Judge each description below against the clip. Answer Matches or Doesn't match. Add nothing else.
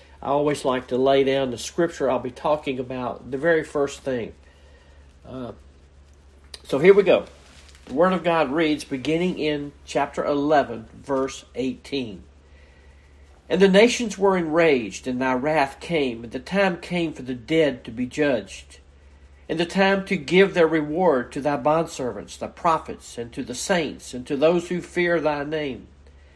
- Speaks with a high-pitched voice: Doesn't match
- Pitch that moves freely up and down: Matches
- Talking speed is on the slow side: Doesn't match